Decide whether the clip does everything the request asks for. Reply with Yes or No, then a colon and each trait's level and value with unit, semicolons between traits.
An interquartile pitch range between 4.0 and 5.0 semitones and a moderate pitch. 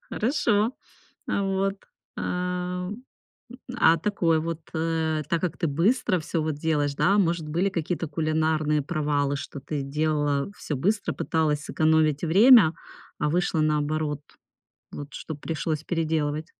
No: average, 2.9 semitones; medium, 160 Hz